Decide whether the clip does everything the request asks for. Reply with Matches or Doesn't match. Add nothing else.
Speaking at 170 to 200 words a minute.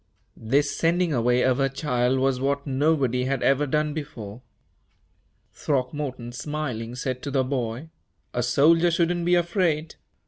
Doesn't match